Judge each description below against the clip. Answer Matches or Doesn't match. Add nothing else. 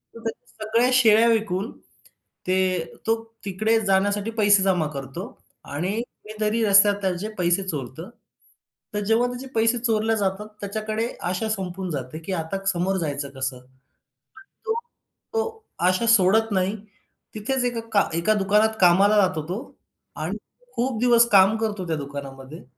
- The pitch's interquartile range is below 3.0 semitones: Doesn't match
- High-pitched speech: Matches